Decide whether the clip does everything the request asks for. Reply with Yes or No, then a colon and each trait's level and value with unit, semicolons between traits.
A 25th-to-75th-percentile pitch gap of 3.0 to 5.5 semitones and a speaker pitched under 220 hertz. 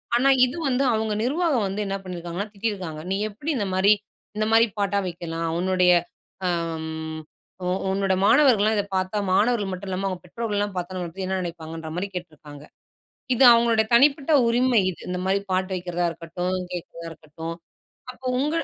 Yes: average, 3.9 semitones; high, 190 Hz